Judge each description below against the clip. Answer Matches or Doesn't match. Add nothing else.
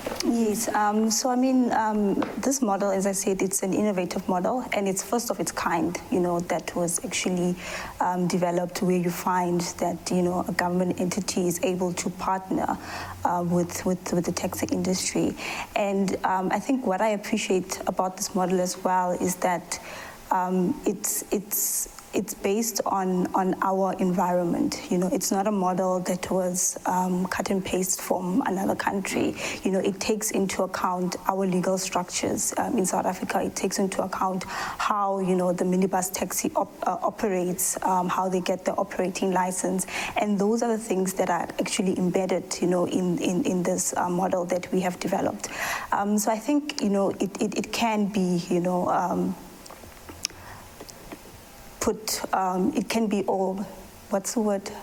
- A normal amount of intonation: Doesn't match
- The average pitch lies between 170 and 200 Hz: Matches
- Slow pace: Doesn't match